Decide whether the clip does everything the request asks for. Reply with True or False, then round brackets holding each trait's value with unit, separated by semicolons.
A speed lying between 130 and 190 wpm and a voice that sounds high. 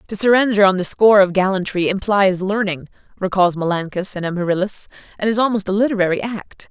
True (170 wpm; 195 Hz)